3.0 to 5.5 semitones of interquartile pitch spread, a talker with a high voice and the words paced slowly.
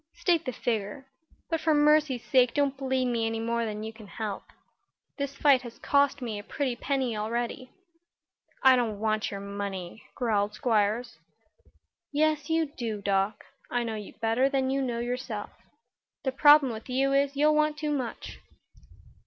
No: average, 4.2 semitones; high, 245 Hz; average, 165 wpm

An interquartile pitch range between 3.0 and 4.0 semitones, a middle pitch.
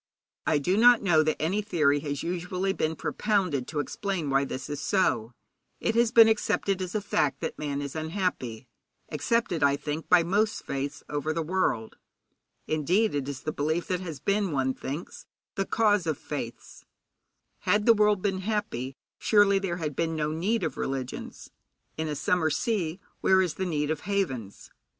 No: average, 5.3 semitones; medium, 165 Hz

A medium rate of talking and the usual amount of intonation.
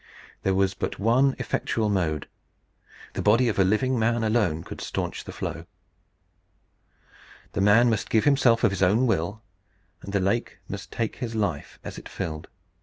Yes: average, 170 wpm; average, 3.3 semitones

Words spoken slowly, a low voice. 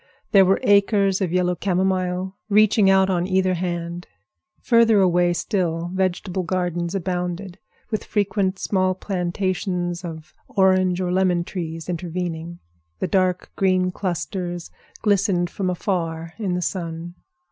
No: slow, 125 wpm; medium, 185 Hz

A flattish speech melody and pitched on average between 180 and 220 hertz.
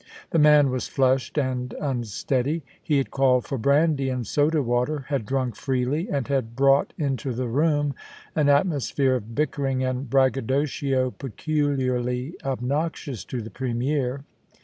No: narrow, 2.3 semitones; low, 135 Hz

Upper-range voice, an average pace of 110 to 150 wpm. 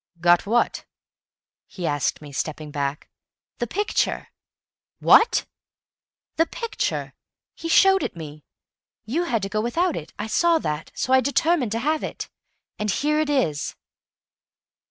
Yes: high, 235 Hz; average, 140 wpm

